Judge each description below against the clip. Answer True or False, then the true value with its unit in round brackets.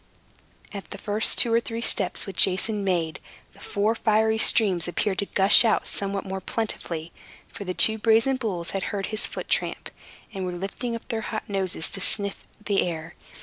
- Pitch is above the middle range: True (200 Hz)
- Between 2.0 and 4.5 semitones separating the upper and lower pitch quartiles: True (2.9 semitones)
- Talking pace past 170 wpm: True (190 wpm)